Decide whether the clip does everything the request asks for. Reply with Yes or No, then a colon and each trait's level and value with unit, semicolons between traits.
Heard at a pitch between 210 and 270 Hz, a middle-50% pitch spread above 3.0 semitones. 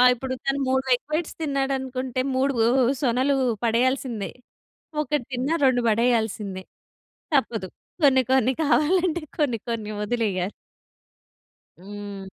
Yes: very high, 255 Hz; average, 3.5 semitones